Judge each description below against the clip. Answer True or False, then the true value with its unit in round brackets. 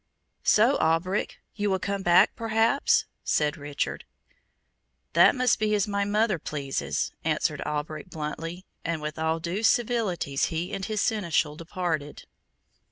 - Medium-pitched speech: True (180 Hz)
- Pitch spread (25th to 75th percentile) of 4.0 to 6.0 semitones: True (5.1 semitones)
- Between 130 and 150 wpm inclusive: True (135 wpm)